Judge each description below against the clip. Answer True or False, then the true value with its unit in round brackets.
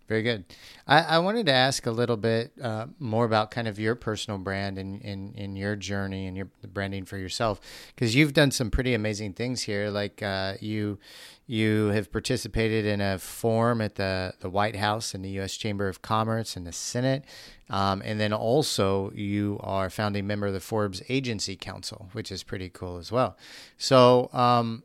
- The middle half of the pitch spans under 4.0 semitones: True (3.0 semitones)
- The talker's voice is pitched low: True (105 Hz)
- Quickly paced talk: False (195 wpm)